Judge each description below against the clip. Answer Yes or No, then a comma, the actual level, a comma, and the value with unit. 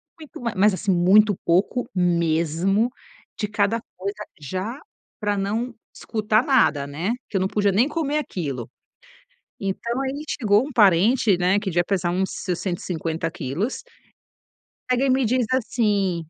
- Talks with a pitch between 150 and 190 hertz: No, high, 200 Hz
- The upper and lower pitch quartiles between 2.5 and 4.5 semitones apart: No, average, 4.9 semitones